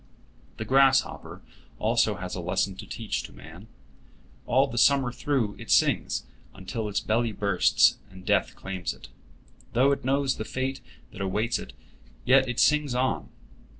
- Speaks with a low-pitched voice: Yes, low, 115 Hz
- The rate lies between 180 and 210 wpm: No, average, 155 wpm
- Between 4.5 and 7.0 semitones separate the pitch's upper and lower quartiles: Yes, wide, 5.4 semitones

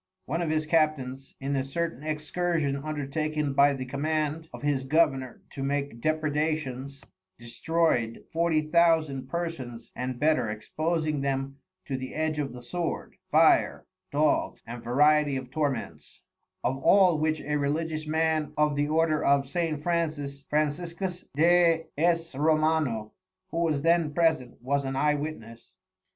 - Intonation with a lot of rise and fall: No, average, 2.8 semitones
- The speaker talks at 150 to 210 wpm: No, average, 140 wpm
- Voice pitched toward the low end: No, medium, 150 Hz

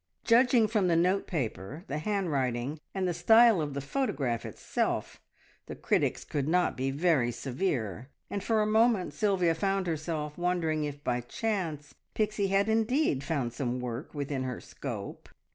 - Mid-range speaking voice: Yes, medium, 160 Hz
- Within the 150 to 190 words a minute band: Yes, average, 160 wpm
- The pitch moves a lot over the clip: Yes, wide, 6.6 semitones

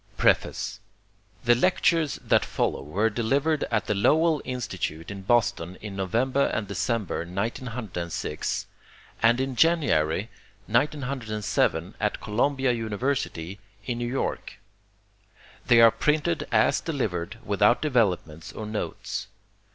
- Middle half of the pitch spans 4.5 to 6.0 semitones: Yes, average, 5.2 semitones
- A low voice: Yes, low, 115 Hz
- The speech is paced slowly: Yes, slow, 110 wpm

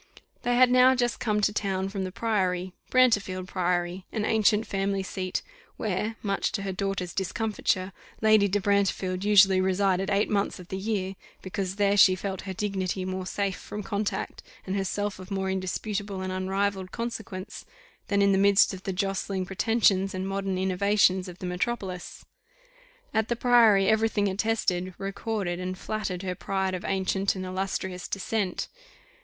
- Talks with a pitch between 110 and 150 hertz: No, high, 195 Hz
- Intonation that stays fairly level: Yes, narrow, 1.8 semitones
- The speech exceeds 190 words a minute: No, average, 165 wpm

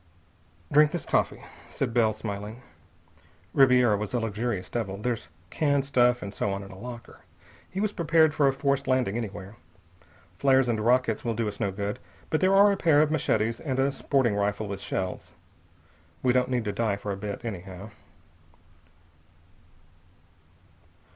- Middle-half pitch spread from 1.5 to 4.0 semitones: No, average, 4.8 semitones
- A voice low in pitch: Yes, low, 120 Hz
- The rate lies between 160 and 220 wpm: Yes, average, 165 wpm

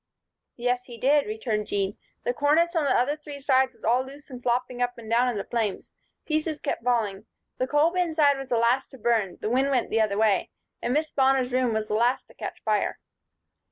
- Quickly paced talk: Yes, fast, 225 wpm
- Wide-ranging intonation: No, average, 3.5 semitones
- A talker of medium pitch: No, very high, 250 Hz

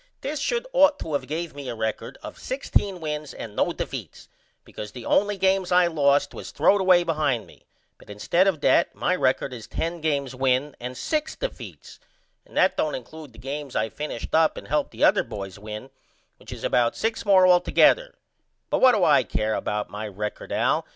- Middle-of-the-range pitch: Yes, medium, 150 Hz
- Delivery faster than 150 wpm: Yes, average, 200 wpm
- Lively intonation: Yes, wide, 6.9 semitones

